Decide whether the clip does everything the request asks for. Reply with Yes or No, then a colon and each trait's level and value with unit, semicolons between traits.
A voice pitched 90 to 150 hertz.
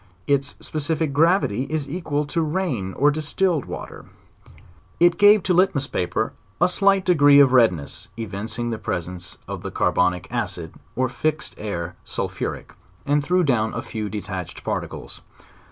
Yes: medium, 140 Hz